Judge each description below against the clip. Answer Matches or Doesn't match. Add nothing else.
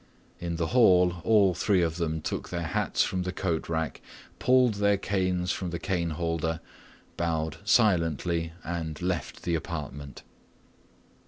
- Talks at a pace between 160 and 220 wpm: Doesn't match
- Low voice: Matches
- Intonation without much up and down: Matches